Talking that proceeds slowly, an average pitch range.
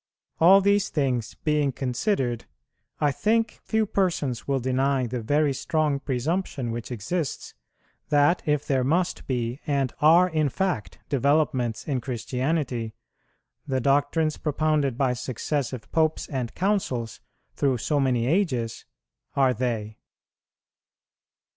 Yes: slow, 120 wpm; average, 4.0 semitones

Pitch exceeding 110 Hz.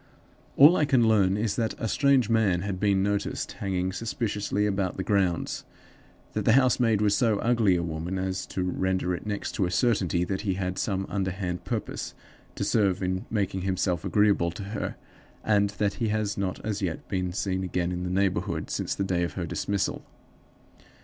No: low, 100 Hz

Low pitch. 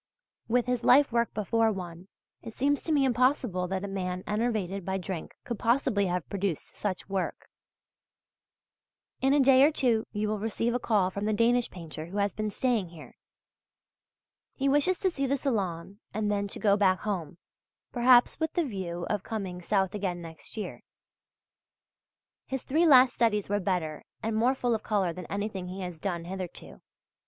No: high, 210 Hz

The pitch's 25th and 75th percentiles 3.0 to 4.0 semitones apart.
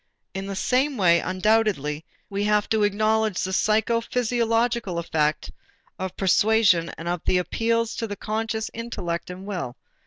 Yes: average, 3.7 semitones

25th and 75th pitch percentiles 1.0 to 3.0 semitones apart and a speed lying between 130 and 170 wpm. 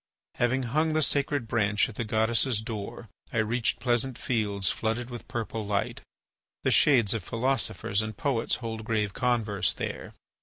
Yes: narrow, 2.5 semitones; average, 155 wpm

